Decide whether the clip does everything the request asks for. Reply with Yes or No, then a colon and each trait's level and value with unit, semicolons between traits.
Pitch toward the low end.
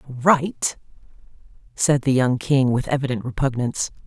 Yes: low, 130 Hz